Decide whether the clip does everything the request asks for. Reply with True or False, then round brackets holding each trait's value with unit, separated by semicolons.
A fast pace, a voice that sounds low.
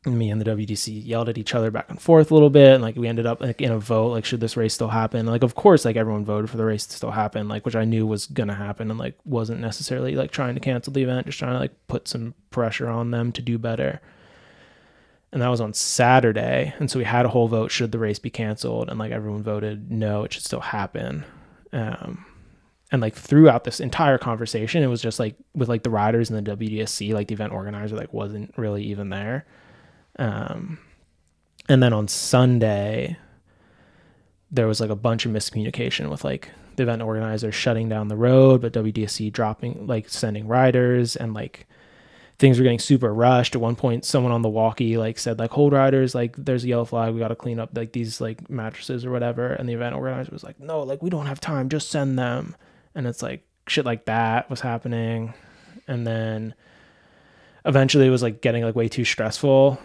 True (220 wpm; 115 Hz)